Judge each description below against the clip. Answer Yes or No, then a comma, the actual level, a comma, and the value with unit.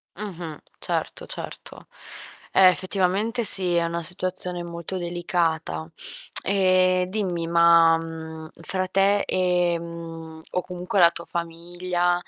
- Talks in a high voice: No, medium, 175 Hz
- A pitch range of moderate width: No, narrow, 1.7 semitones